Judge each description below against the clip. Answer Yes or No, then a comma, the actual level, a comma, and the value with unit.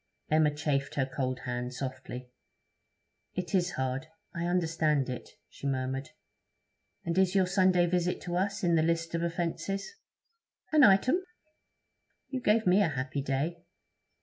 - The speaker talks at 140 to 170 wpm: Yes, average, 145 wpm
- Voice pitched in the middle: Yes, medium, 165 Hz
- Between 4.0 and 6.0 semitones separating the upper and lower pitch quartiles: Yes, average, 5.1 semitones